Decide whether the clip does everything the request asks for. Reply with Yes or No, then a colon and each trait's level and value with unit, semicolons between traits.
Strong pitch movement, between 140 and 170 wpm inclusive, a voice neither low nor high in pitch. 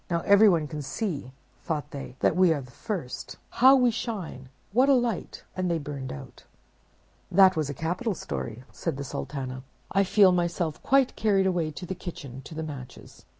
No: wide, 5.9 semitones; average, 180 wpm; medium, 170 Hz